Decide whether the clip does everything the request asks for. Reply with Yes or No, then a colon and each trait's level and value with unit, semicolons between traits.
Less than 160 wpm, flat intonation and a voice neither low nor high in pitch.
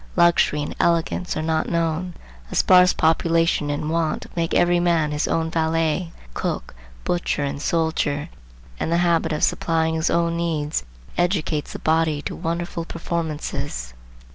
Yes: average, 145 wpm; narrow, 1.5 semitones; medium, 165 Hz